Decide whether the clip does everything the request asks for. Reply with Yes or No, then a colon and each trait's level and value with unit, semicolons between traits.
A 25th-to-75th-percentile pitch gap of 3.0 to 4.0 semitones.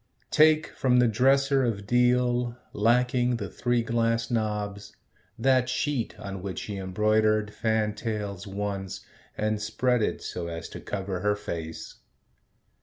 Yes: average, 3.3 semitones